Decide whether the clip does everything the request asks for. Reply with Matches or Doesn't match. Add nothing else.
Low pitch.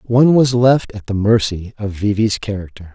Matches